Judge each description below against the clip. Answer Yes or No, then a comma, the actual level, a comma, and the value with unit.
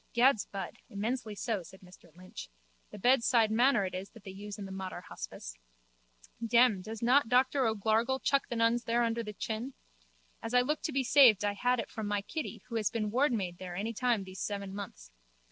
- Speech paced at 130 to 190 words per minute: No, fast, 205 wpm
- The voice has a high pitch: Yes, high, 220 Hz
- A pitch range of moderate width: Yes, average, 3.7 semitones